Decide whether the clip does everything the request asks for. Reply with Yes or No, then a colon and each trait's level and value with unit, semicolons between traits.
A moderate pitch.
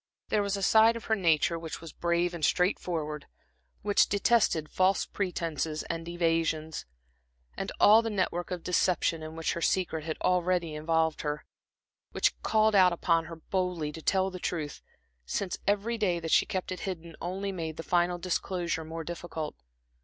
Yes: medium, 175 Hz